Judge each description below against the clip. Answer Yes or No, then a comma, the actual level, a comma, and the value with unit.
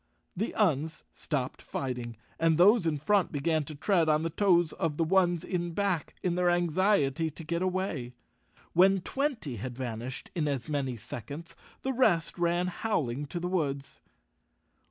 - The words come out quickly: No, average, 165 wpm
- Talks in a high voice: No, medium, 165 Hz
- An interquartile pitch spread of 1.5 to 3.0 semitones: No, average, 4.3 semitones